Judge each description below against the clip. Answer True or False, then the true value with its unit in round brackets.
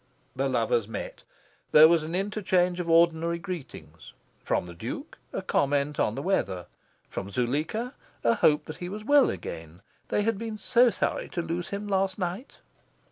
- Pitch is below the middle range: False (175 Hz)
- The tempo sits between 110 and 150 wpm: False (170 wpm)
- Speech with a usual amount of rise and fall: False (6.2 semitones)